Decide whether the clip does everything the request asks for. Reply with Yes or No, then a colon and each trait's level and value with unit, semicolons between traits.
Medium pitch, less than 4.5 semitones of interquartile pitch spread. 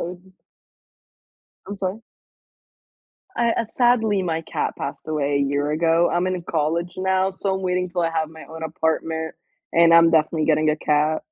Yes: medium, 165 Hz; average, 2.8 semitones